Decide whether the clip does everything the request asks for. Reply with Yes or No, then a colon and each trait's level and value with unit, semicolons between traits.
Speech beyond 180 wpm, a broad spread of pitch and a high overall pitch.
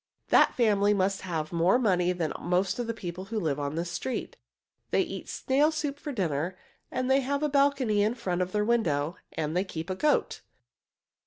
Yes: average, 190 wpm; wide, 6.3 semitones; high, 195 Hz